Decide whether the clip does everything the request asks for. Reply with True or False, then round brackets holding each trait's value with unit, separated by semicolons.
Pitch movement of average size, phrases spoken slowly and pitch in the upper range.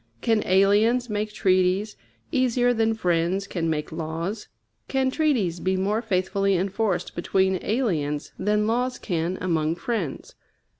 True (4.1 semitones; 130 wpm; 195 Hz)